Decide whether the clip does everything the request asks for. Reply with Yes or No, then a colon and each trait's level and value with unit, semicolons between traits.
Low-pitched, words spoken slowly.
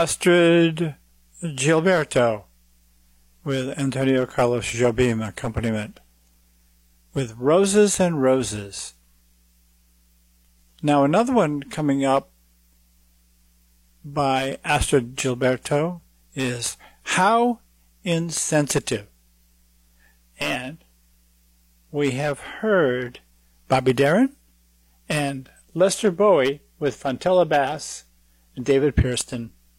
Yes: low, 125 Hz; slow, 75 wpm